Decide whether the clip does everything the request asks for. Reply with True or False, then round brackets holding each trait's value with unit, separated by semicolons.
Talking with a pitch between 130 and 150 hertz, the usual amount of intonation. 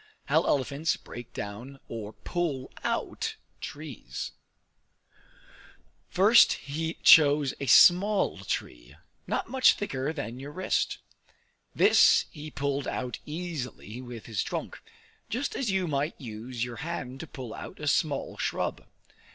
True (140 Hz; 4.7 semitones)